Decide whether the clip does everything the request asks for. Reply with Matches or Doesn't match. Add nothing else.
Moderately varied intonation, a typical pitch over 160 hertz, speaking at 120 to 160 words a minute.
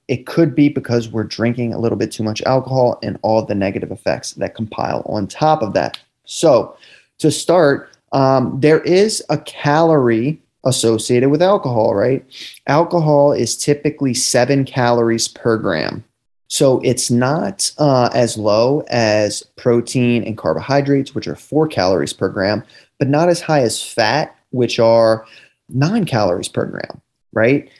Doesn't match